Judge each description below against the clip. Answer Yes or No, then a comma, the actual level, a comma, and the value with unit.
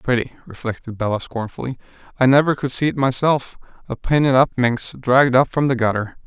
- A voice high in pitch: No, low, 130 Hz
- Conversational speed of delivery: Yes, average, 180 wpm